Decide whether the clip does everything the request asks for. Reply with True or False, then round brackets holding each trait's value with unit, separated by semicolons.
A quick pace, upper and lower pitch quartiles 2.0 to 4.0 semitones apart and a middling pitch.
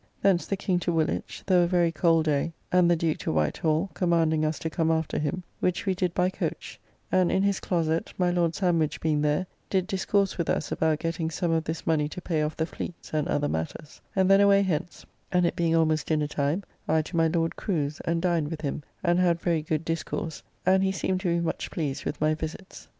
True (230 wpm; 2.6 semitones; 165 Hz)